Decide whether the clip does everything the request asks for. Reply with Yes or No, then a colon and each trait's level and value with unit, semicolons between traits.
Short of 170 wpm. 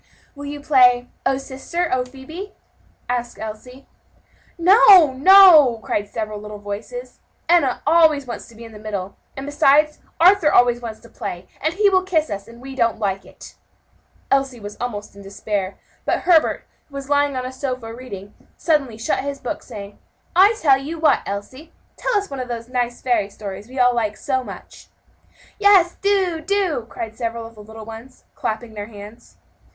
No: average, 180 wpm